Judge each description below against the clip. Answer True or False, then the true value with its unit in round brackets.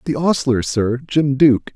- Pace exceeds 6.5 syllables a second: False (4.9 syllables/s)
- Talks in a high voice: False (135 Hz)